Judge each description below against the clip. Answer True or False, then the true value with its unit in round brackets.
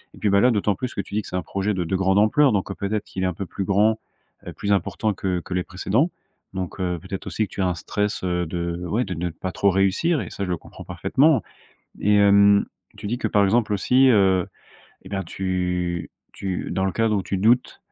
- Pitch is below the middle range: True (100 Hz)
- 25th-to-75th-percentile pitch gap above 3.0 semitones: False (2.5 semitones)